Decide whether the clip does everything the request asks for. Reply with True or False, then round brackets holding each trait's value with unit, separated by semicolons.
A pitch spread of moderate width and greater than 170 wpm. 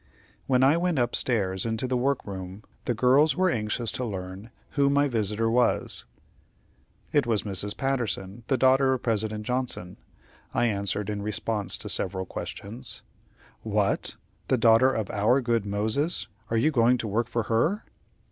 False (3.9 semitones; 160 wpm)